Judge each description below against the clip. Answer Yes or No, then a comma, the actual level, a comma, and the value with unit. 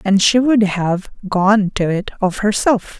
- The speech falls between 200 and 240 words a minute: No, average, 180 wpm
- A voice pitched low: No, high, 200 Hz